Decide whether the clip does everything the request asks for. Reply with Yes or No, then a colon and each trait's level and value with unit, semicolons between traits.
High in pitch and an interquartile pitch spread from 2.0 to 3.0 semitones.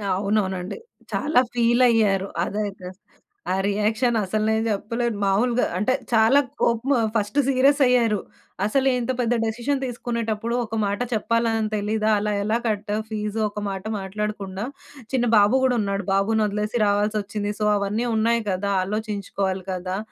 Yes: high, 215 Hz; narrow, 2.5 semitones